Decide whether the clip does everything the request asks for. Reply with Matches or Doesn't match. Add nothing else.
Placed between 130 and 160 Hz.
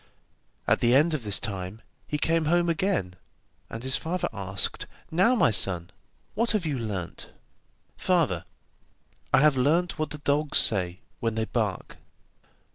Matches